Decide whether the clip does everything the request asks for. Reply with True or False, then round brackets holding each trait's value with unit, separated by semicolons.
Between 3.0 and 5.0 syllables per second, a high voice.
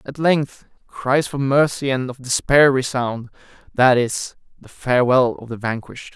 False (4.4 syllables/s; 130 Hz)